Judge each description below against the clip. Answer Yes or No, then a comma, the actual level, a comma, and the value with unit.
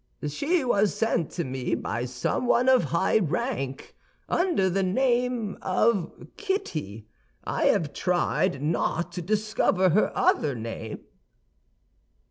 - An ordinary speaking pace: No, slow, 115 wpm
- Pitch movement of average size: No, wide, 7.6 semitones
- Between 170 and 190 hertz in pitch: Yes, medium, 185 Hz